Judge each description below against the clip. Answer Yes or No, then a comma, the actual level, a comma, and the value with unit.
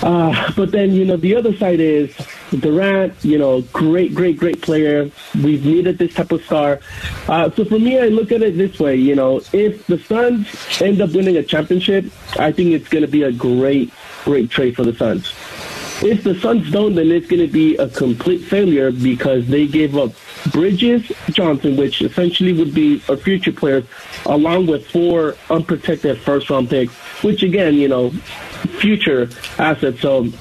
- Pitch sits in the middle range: Yes, medium, 165 Hz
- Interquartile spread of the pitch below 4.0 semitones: No, average, 5.3 semitones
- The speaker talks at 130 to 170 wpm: No, average, 185 wpm